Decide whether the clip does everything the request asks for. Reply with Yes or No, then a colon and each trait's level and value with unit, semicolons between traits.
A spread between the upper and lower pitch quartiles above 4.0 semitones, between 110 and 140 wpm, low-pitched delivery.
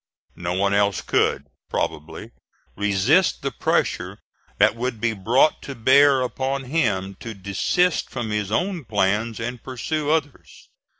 Yes: wide, 5.4 semitones; slow, 135 wpm; low, 115 Hz